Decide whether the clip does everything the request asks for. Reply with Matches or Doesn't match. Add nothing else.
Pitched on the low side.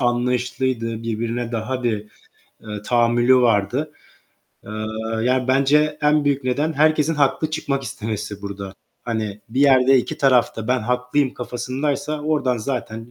Matches